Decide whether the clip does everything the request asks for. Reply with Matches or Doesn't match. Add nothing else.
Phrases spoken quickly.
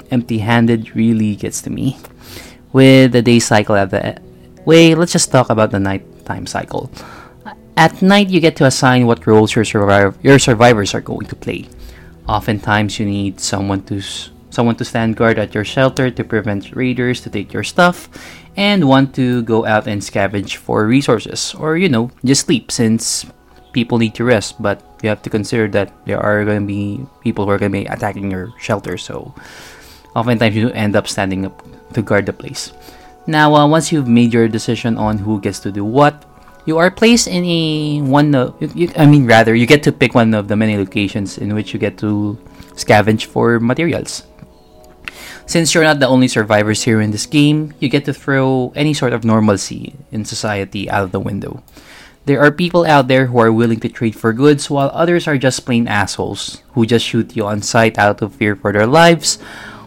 Matches